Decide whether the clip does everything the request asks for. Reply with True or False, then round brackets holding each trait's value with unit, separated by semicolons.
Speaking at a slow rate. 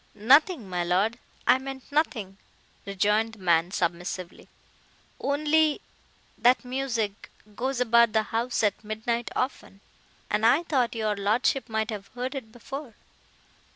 True (120 wpm)